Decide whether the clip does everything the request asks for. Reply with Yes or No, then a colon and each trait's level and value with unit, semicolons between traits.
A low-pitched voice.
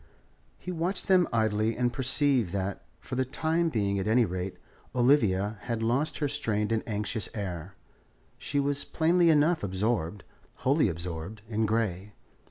Yes: low, 115 Hz